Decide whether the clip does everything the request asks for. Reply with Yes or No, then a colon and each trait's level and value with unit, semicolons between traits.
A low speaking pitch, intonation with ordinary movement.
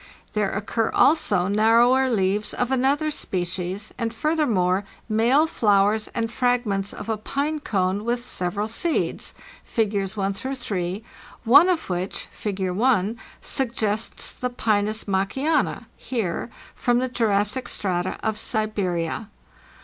No: high, 215 Hz; average, 4.0 semitones